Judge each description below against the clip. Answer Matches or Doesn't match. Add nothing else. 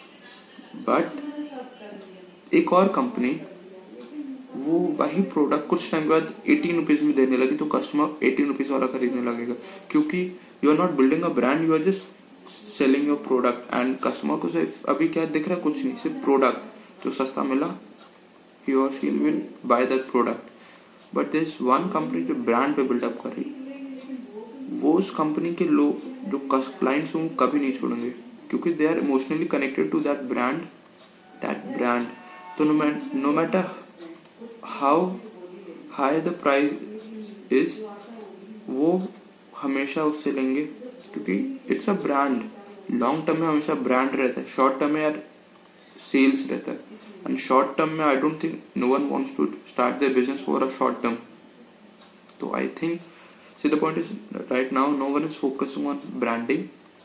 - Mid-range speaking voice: Matches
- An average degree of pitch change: Doesn't match